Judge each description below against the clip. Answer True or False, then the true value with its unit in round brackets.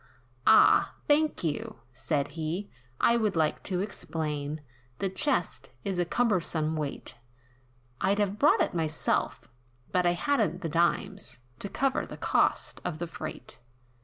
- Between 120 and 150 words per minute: True (140 wpm)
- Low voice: False (175 Hz)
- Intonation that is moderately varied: True (4.7 semitones)